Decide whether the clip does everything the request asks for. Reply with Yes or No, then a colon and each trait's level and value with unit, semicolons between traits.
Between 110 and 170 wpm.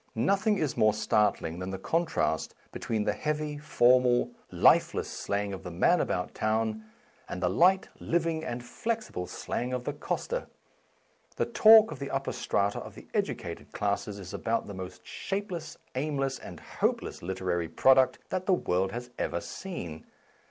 Yes: average, 160 wpm